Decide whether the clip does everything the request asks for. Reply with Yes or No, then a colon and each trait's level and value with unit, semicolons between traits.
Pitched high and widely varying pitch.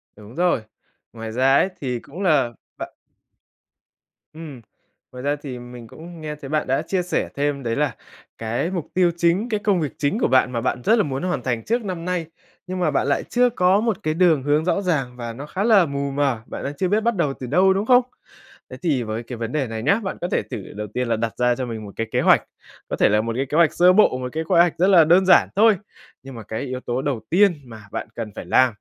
No: medium, 145 Hz; wide, 6.4 semitones